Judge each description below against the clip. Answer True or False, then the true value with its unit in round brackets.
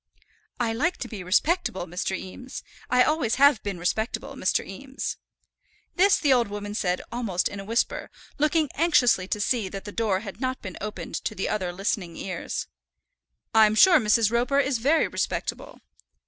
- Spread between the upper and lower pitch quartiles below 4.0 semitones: False (5.0 semitones)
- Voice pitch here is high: True (225 Hz)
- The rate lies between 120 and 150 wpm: False (165 wpm)